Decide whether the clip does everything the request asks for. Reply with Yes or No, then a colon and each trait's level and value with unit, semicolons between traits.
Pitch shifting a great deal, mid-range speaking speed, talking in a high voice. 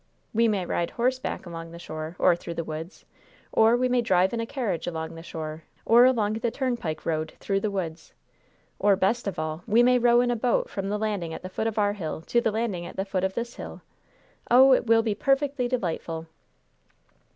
No: wide, 5.8 semitones; fast, 220 wpm; high, 205 Hz